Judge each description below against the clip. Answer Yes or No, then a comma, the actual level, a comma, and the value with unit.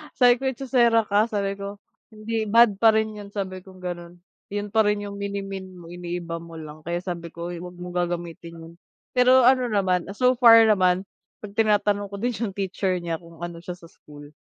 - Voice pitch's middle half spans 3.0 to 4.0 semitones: Yes, average, 3.7 semitones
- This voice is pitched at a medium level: No, high, 195 Hz